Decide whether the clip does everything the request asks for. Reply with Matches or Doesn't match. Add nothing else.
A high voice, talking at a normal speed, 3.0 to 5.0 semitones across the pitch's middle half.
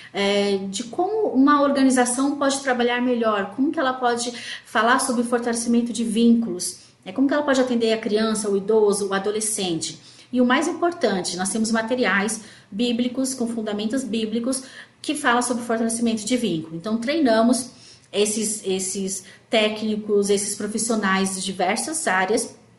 Matches